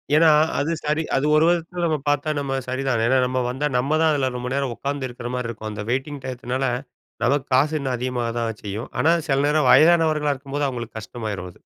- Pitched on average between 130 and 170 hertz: Yes, low, 135 Hz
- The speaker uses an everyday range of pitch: Yes, average, 3.3 semitones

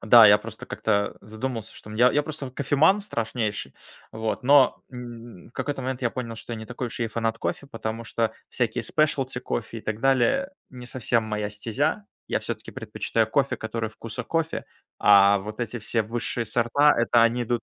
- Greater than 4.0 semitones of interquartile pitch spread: No, average, 2.8 semitones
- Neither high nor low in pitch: No, low, 115 Hz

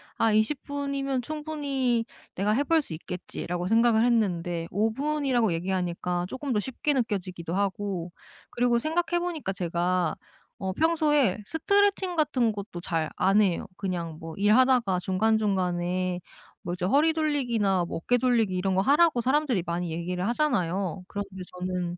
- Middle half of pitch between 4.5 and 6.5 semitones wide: No, wide, 7.1 semitones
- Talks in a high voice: Yes, high, 210 Hz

